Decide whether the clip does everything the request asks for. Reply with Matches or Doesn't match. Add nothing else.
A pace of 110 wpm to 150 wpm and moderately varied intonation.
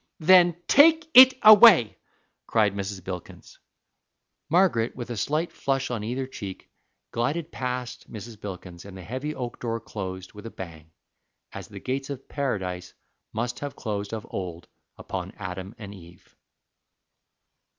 Doesn't match